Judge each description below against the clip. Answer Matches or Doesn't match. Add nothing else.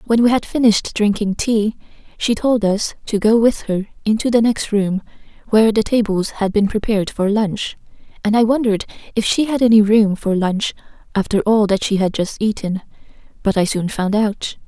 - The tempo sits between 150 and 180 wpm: Doesn't match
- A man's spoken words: Doesn't match